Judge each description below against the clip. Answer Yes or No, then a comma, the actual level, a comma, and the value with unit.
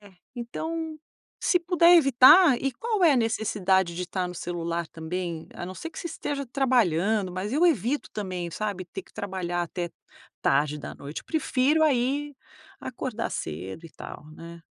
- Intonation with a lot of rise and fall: Yes, wide, 8.3 semitones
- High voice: Yes, high, 210 Hz